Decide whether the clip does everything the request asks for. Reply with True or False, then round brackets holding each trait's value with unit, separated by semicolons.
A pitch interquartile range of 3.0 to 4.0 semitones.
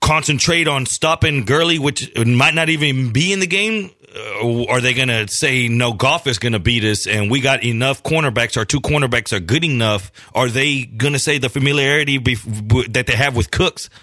True (3.5 semitones)